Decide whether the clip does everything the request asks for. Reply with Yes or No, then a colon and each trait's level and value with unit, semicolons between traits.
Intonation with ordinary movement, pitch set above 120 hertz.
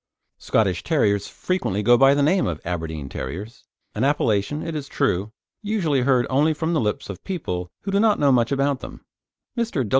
No: wide, 7.5 semitones; low, 135 Hz